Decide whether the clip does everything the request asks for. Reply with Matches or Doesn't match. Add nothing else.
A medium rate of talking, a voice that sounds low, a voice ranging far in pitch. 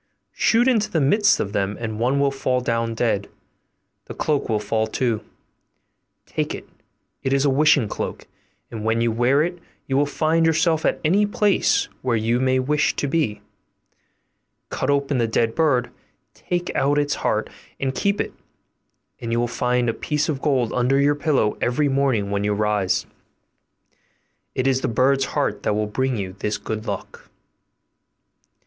Doesn't match